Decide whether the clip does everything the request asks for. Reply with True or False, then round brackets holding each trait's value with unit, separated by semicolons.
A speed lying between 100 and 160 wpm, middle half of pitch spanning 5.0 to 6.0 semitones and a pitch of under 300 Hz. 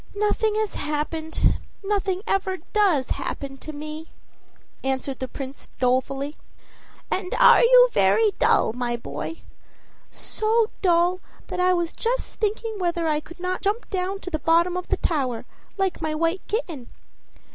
False (145 wpm; 5.4 semitones; 345 Hz)